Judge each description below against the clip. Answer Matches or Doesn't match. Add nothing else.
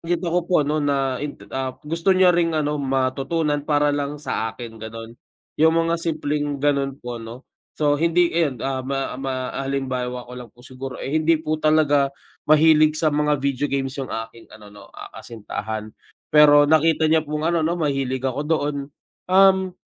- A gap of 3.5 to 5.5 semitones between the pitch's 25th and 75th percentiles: Doesn't match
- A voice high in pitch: Doesn't match